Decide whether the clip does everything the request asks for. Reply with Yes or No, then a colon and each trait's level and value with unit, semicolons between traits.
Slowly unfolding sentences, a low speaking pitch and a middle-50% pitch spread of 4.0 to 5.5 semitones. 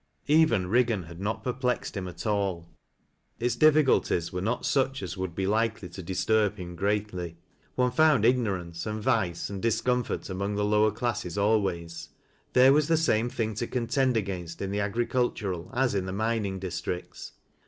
No: average, 175 wpm; low, 105 Hz; average, 4.5 semitones